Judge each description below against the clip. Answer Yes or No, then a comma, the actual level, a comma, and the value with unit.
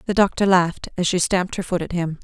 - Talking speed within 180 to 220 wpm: No, fast, 270 wpm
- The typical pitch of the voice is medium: Yes, medium, 180 Hz